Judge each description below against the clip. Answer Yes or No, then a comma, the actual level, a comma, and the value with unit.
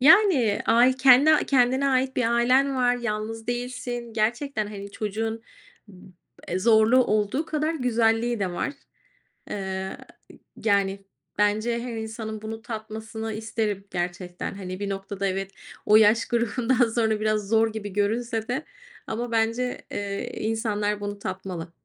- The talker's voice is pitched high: Yes, high, 220 Hz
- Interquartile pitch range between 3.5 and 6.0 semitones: No, average, 3.0 semitones